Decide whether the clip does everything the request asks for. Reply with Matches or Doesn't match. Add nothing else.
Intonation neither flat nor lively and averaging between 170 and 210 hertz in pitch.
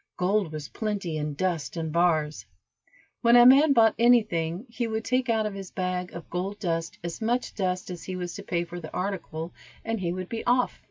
Matches